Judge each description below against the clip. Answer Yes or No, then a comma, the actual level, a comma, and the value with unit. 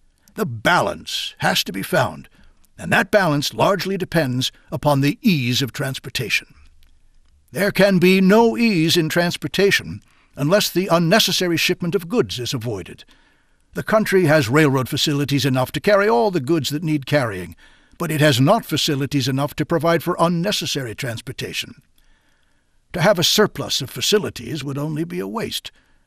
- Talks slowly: No, average, 155 wpm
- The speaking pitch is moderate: Yes, medium, 155 Hz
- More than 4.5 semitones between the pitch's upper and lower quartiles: Yes, average, 5.2 semitones